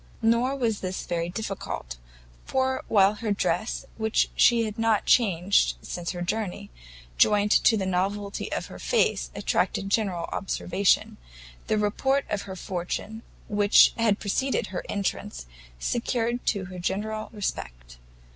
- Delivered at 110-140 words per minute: Yes, slow, 135 wpm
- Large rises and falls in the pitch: No, average, 3.4 semitones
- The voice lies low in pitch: No, high, 205 Hz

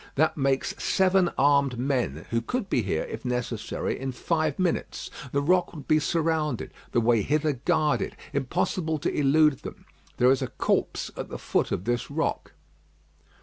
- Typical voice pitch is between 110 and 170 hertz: Yes, medium, 140 Hz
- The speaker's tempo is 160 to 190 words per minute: Yes, average, 165 wpm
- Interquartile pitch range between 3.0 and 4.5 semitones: Yes, average, 4.2 semitones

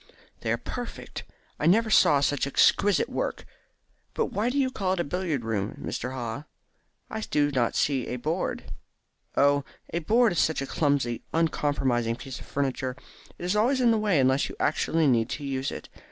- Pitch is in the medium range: Yes, medium, 145 Hz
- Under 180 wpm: No, average, 185 wpm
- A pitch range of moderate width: No, wide, 6.6 semitones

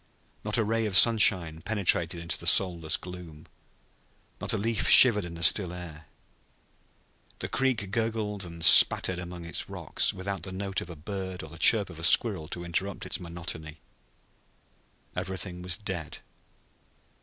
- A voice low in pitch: Yes, very low, 90 Hz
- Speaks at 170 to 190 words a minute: No, average, 155 wpm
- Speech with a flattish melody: No, average, 3.3 semitones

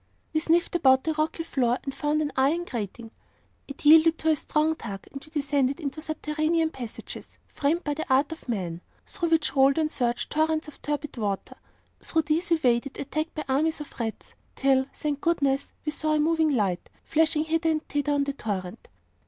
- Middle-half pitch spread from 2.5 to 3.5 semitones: Yes, average, 3.1 semitones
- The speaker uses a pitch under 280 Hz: No, very high, 295 Hz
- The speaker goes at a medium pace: Yes, average, 195 wpm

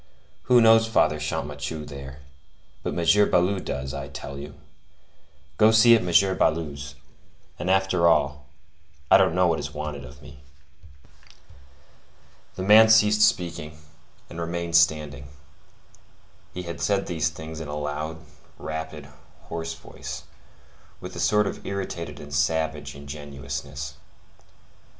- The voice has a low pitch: Yes, very low, 80 Hz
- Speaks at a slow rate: Yes, slow, 130 wpm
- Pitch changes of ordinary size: Yes, average, 4.0 semitones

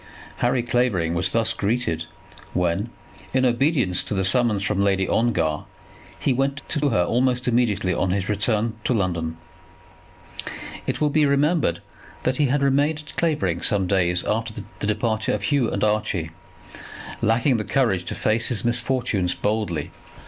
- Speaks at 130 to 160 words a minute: Yes, average, 155 wpm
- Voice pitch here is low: Yes, low, 110 Hz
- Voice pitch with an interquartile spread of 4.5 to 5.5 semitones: Yes, average, 5.1 semitones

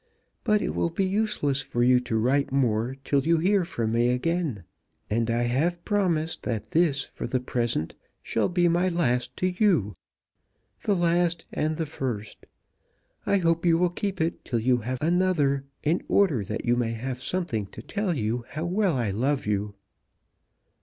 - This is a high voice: No, medium, 145 Hz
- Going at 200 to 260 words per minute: No, average, 175 wpm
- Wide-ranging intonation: Yes, wide, 6.5 semitones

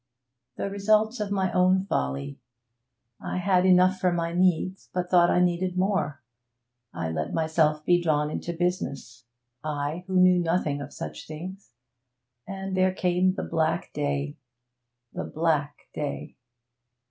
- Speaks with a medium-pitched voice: Yes, medium, 175 Hz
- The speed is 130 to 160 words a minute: Yes, average, 140 wpm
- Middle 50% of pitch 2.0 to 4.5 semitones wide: Yes, average, 3.6 semitones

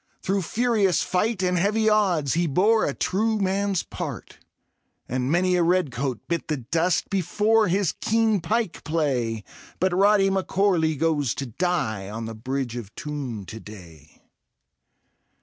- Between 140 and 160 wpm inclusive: Yes, average, 150 wpm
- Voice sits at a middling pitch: Yes, medium, 175 Hz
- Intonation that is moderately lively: No, wide, 7.0 semitones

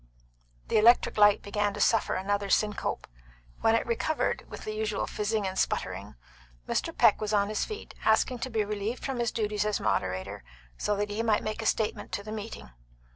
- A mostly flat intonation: Yes, narrow, 1.5 semitones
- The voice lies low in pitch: No, high, 210 Hz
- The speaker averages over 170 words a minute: Yes, average, 190 wpm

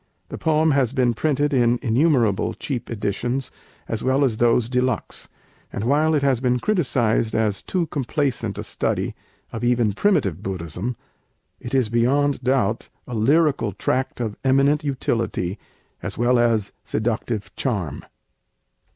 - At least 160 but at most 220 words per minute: No, average, 140 wpm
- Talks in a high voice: No, low, 120 Hz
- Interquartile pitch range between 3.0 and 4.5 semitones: Yes, average, 3.8 semitones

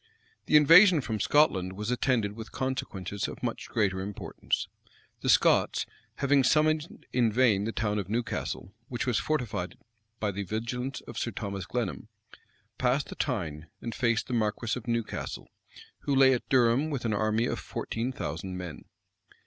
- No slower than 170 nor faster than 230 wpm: No, average, 160 wpm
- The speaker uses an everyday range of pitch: Yes, average, 4.1 semitones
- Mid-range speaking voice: No, low, 115 Hz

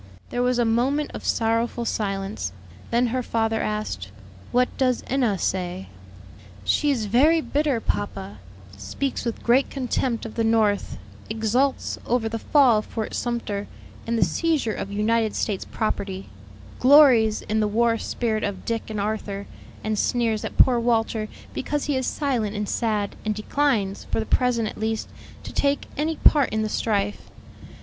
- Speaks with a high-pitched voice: Yes, high, 225 Hz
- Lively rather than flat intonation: No, average, 2.9 semitones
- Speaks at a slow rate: No, average, 160 wpm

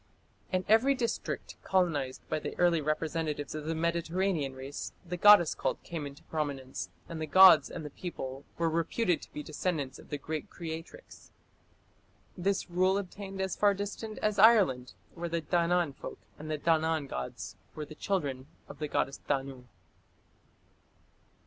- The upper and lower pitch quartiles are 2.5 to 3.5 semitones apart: No, average, 4.2 semitones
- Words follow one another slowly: No, average, 155 wpm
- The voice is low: No, medium, 165 Hz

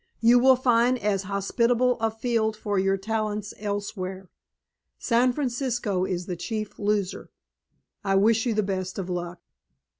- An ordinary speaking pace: Yes, average, 145 wpm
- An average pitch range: Yes, average, 3.3 semitones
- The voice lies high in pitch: Yes, high, 210 Hz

